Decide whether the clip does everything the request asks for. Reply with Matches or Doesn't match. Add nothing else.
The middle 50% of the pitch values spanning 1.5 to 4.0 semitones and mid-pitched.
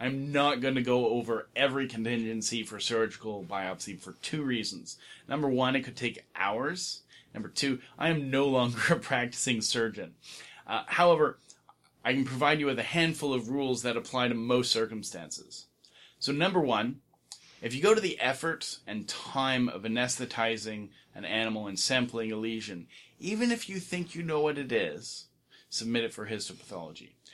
Doesn't match